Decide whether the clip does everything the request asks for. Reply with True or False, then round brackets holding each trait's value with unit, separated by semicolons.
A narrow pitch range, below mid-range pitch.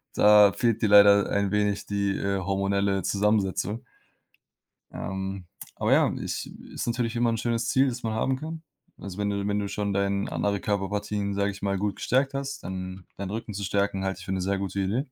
True (2.0 semitones; 100 Hz)